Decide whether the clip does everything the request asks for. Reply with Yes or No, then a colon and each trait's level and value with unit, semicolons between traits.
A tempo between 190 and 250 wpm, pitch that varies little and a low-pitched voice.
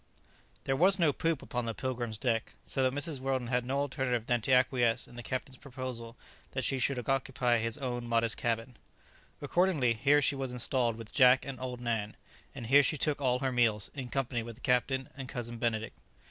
Yes: average, 200 wpm; narrow, 2.3 semitones; low, 125 Hz